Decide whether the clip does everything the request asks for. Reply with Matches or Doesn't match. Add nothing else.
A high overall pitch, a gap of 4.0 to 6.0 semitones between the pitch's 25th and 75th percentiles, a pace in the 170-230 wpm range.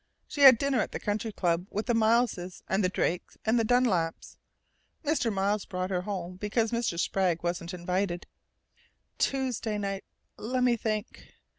Doesn't match